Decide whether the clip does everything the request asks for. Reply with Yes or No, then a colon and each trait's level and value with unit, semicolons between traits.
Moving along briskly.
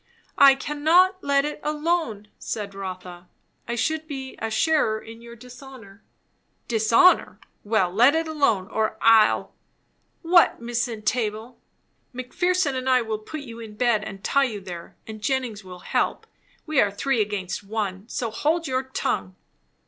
No: average, 155 wpm